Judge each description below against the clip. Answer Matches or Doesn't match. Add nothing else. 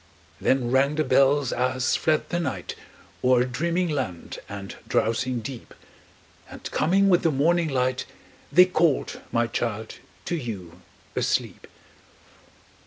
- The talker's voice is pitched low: Matches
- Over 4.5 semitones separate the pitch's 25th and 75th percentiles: Matches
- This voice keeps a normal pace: Doesn't match